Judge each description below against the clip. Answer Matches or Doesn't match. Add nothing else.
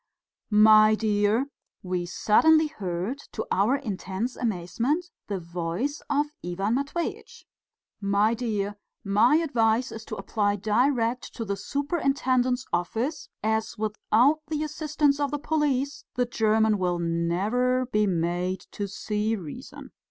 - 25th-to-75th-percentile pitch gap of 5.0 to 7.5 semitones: Matches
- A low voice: Doesn't match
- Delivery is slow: Matches